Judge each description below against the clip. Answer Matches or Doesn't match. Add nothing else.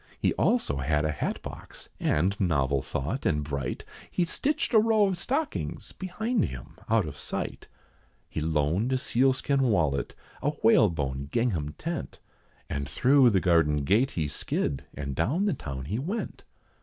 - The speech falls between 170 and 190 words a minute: Doesn't match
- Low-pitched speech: Matches